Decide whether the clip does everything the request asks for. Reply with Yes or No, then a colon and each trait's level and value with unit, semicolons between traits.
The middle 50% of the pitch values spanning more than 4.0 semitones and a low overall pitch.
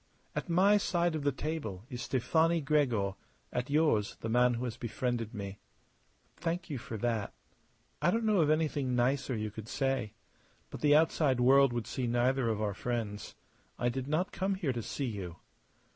Yes: average, 5.1 semitones; low, 130 Hz